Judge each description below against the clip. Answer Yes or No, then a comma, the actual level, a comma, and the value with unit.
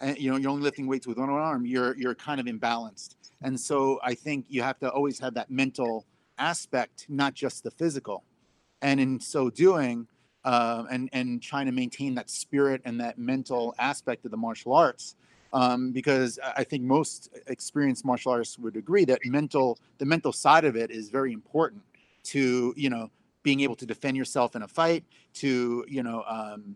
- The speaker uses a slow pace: No, average, 195 wpm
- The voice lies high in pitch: No, low, 130 Hz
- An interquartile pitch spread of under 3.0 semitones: Yes, narrow, 2.4 semitones